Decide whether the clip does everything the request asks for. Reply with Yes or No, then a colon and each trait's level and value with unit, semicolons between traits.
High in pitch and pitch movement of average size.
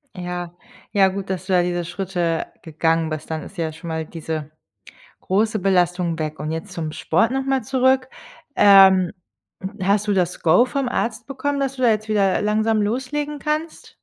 No: high, 195 Hz; wide, 5.7 semitones